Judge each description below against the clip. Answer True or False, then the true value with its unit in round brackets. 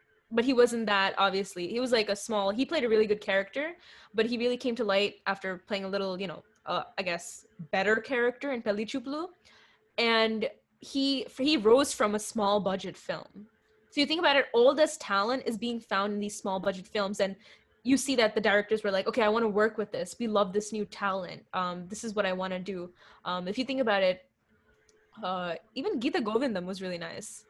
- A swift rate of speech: True (225 wpm)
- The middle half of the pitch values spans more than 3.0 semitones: True (3.5 semitones)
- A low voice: False (210 Hz)